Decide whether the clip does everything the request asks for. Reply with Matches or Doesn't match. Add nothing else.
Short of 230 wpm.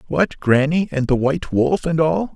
Matches